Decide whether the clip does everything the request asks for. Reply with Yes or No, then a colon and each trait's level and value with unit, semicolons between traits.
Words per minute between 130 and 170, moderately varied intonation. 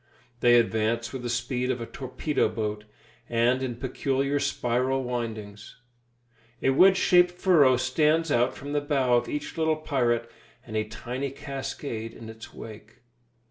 Yes: average, 150 wpm; average, 3.2 semitones